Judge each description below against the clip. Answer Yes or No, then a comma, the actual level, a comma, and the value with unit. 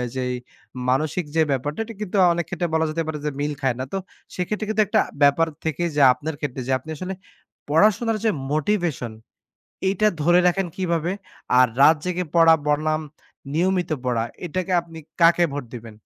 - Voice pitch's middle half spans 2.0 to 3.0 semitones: No, average, 3.7 semitones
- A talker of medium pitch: Yes, medium, 165 Hz